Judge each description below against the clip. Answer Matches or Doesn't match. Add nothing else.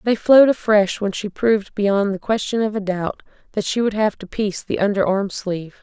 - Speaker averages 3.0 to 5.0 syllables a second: Doesn't match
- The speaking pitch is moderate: Doesn't match